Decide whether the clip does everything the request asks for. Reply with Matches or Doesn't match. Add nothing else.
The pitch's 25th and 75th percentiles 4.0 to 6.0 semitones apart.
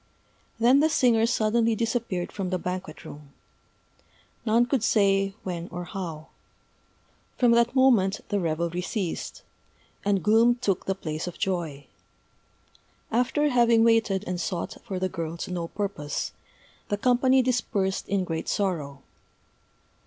Matches